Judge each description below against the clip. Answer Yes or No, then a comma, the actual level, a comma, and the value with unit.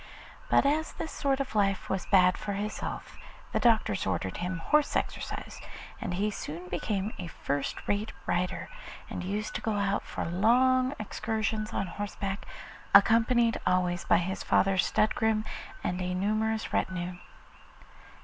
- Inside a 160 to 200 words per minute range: No, average, 150 wpm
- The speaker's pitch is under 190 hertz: No, high, 205 Hz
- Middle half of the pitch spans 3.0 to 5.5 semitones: Yes, average, 3.4 semitones